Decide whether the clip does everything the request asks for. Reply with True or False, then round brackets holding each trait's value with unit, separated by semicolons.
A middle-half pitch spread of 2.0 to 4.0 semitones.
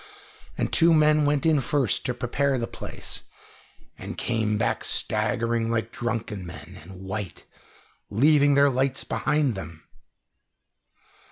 False (5.1 semitones)